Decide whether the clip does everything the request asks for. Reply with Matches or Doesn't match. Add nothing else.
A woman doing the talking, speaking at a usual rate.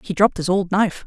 Doesn't match